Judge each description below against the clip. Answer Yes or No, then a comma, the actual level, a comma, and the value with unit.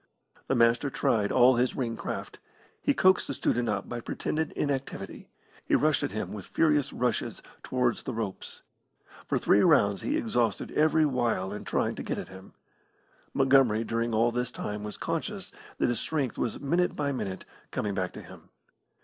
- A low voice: Yes, low, 120 Hz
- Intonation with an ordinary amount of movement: Yes, average, 4.6 semitones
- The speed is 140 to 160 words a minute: No, average, 175 wpm